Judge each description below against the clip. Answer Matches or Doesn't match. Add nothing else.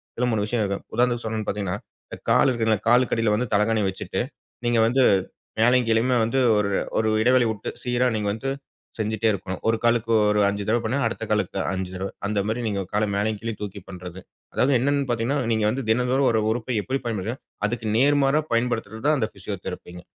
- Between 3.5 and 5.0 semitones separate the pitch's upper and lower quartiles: Doesn't match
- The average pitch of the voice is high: Doesn't match